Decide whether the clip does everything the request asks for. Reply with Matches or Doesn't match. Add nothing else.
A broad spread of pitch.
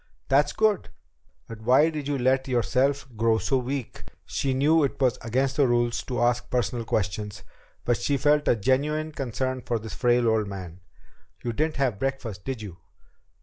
Doesn't match